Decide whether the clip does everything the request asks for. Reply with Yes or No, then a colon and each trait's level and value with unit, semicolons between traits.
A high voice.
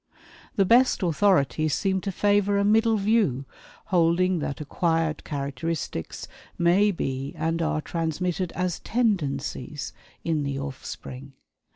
No: medium, 170 Hz